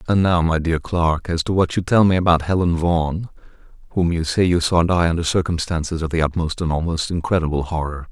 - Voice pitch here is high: No, very low, 85 Hz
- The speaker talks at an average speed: No, fast, 215 wpm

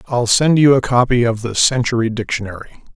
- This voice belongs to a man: Yes, male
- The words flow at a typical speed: Yes, average, 185 wpm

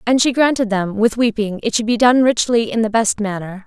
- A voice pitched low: No, high, 225 Hz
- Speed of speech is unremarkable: No, fast, 245 wpm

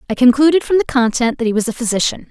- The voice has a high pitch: Yes, very high, 255 Hz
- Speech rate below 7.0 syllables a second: No, 7.1 syllables/s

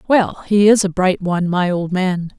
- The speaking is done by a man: No, female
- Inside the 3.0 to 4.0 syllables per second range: No, 4.6 syllables/s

